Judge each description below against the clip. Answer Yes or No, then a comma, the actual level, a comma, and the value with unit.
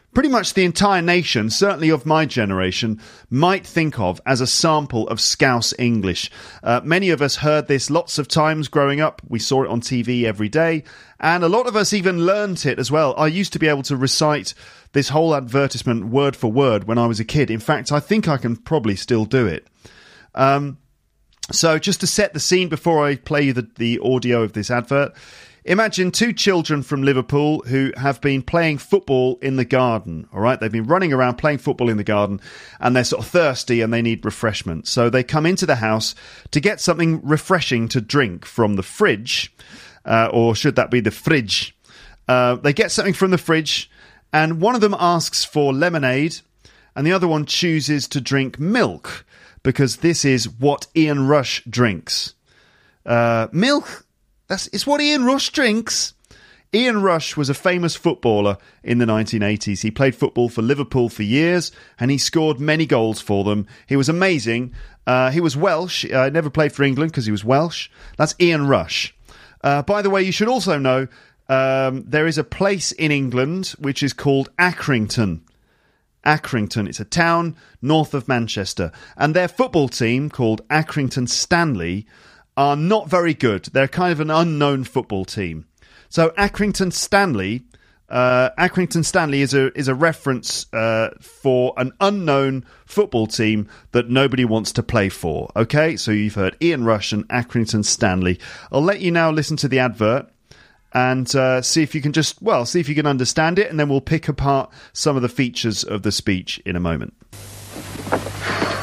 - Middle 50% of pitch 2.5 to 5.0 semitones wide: No, wide, 5.6 semitones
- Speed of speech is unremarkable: Yes, average, 190 wpm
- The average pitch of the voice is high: No, medium, 140 Hz